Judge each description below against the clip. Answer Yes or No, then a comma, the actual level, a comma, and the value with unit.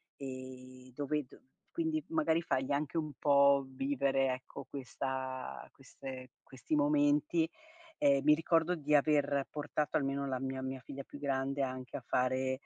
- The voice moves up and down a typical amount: No, narrow, 2.1 semitones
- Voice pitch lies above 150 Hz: No, medium, 140 Hz